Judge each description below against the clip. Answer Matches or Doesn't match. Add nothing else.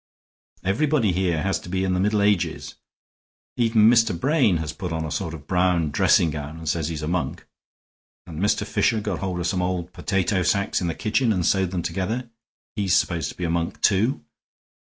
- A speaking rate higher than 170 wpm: Matches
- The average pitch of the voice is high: Doesn't match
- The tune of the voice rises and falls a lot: Doesn't match